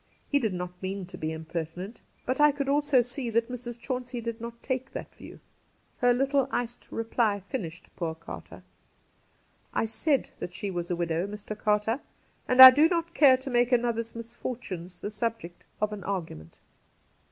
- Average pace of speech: Yes, average, 175 wpm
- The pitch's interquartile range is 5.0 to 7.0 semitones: Yes, wide, 5.5 semitones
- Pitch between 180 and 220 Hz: No, high, 230 Hz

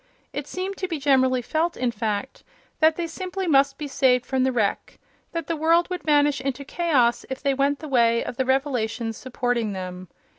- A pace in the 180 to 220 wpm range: Yes, average, 190 wpm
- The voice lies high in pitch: Yes, very high, 270 Hz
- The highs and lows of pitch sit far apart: No, average, 4.4 semitones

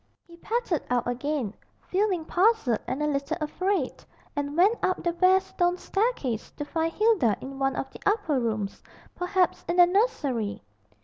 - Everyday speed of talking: Yes, average, 165 wpm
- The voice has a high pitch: Yes, very high, 330 Hz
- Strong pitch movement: Yes, wide, 5.8 semitones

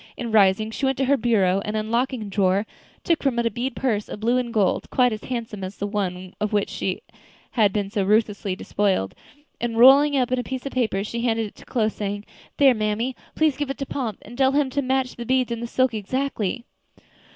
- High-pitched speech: Yes, high, 230 Hz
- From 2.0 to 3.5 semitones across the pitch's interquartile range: No, average, 3.9 semitones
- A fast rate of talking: Yes, fast, 235 wpm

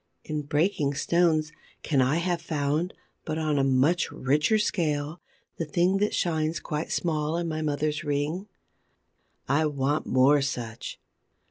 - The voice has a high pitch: No, medium, 155 Hz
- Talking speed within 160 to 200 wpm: No, average, 140 wpm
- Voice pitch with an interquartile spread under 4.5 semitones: Yes, average, 2.7 semitones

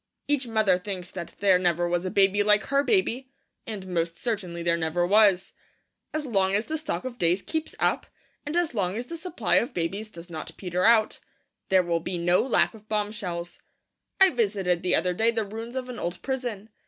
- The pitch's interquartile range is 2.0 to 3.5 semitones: No, average, 5.0 semitones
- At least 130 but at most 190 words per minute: No, fast, 205 wpm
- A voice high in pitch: Yes, high, 205 Hz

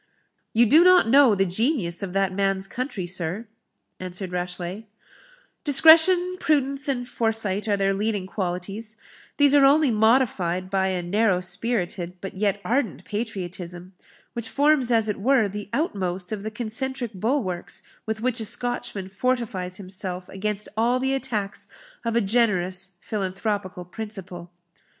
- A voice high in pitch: Yes, high, 210 Hz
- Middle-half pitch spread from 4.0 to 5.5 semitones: Yes, average, 4.6 semitones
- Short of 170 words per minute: Yes, average, 140 wpm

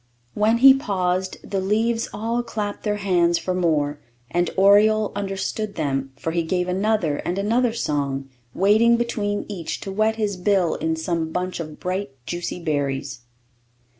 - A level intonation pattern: No, average, 4.3 semitones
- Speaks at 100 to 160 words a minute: Yes, average, 155 wpm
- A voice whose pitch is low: No, high, 190 Hz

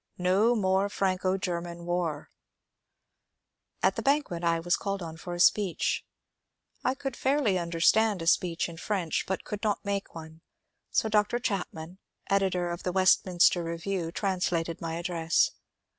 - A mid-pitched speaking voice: Yes, medium, 180 Hz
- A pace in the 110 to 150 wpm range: Yes, average, 145 wpm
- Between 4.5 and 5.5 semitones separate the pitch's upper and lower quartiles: No, average, 2.8 semitones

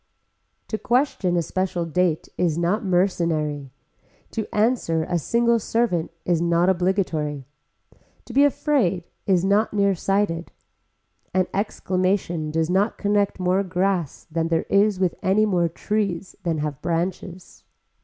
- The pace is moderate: No, slow, 130 wpm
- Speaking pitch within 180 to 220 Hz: Yes, medium, 185 Hz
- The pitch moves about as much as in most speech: Yes, average, 3.2 semitones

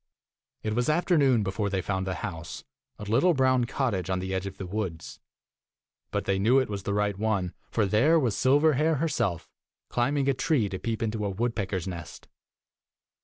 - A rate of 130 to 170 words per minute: No, average, 180 wpm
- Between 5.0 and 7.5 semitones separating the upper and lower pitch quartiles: Yes, wide, 5.4 semitones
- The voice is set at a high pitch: No, low, 105 Hz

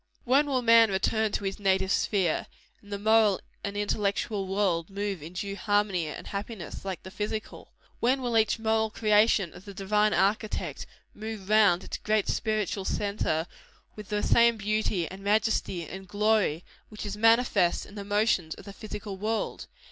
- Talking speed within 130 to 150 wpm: No, average, 170 wpm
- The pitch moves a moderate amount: No, narrow, 2.1 semitones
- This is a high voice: Yes, high, 205 Hz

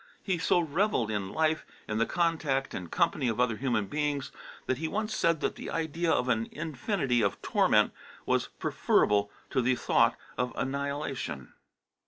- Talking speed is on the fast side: No, average, 165 wpm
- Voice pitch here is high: No, medium, 140 Hz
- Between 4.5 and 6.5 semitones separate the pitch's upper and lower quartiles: Yes, average, 5.3 semitones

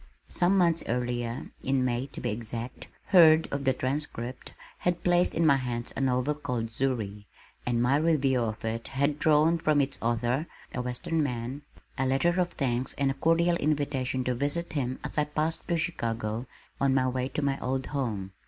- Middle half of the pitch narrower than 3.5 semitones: No, average, 3.8 semitones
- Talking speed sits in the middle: Yes, average, 185 wpm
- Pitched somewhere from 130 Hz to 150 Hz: Yes, low, 135 Hz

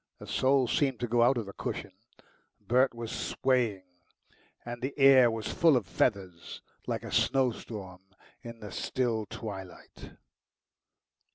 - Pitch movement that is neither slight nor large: Yes, average, 3.6 semitones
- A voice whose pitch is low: Yes, low, 120 Hz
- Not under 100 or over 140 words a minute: Yes, slow, 135 wpm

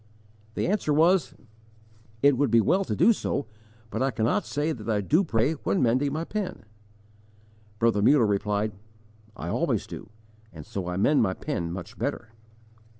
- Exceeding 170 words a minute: No, average, 165 wpm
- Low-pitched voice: Yes, low, 120 Hz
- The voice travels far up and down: Yes, wide, 6.5 semitones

